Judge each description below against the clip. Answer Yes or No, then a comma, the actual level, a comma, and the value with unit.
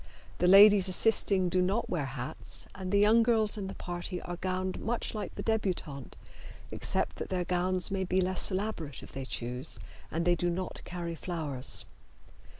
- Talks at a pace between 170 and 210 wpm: Yes, average, 175 wpm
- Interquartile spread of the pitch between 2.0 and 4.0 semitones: Yes, narrow, 2.5 semitones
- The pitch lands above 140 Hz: Yes, medium, 185 Hz